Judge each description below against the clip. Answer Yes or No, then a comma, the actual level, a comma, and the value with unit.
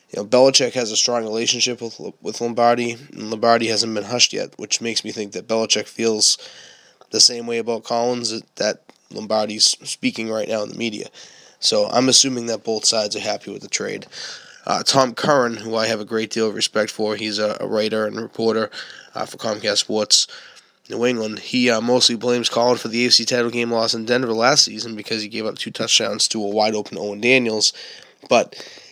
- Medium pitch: No, low, 115 Hz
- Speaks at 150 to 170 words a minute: No, average, 200 wpm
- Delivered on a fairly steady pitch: Yes, narrow, 1.7 semitones